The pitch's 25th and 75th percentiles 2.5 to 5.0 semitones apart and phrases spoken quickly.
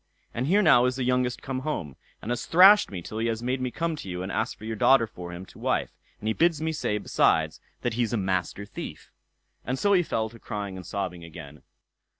No: wide, 5.5 semitones; fast, 240 wpm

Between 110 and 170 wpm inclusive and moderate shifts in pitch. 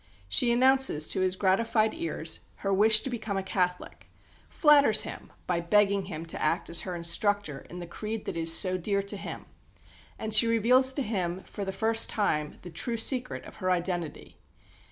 No: average, 185 wpm; average, 4.1 semitones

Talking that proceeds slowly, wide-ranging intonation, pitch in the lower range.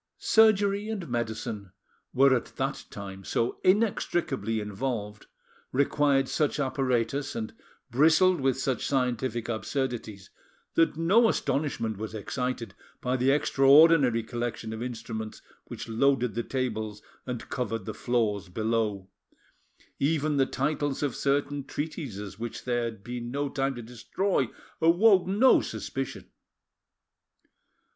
No: slow, 120 wpm; average, 4.3 semitones; low, 125 Hz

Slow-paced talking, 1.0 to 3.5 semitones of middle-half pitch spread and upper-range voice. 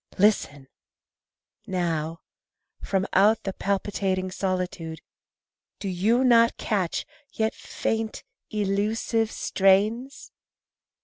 Yes: slow, 80 wpm; average, 3.0 semitones; high, 195 Hz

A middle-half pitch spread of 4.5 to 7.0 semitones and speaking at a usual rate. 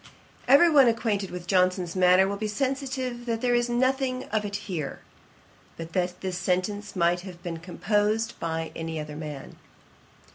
Yes: average, 5.3 semitones; average, 160 wpm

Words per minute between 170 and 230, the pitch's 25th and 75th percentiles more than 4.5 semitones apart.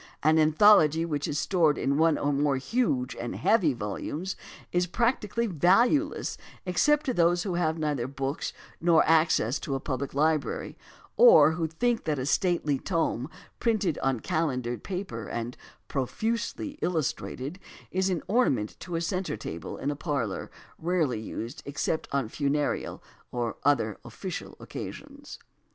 No: average, 145 wpm; average, 5.1 semitones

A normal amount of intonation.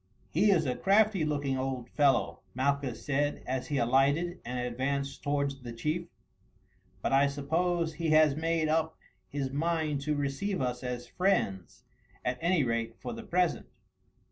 Yes: average, 3.8 semitones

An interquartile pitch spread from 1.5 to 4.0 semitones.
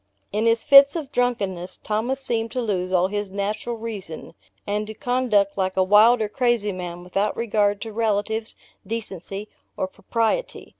Yes: average, 2.7 semitones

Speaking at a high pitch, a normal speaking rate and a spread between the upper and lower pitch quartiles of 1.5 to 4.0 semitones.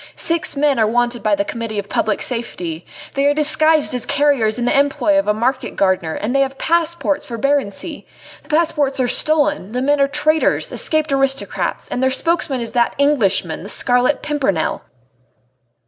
No: very high, 270 Hz; average, 180 wpm; average, 4.5 semitones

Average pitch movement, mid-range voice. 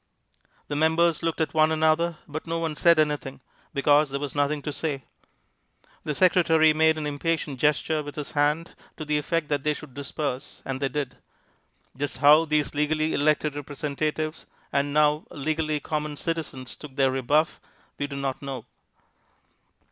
No: narrow, 1.7 semitones; medium, 150 Hz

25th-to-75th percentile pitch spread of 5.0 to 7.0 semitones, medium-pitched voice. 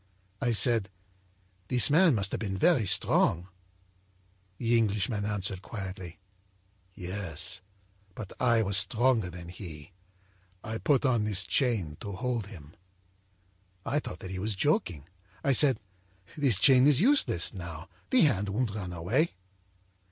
No: average, 5.3 semitones; low, 105 Hz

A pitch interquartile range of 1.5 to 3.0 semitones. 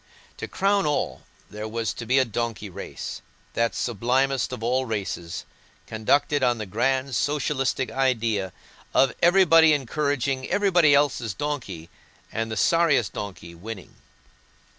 No: average, 4.5 semitones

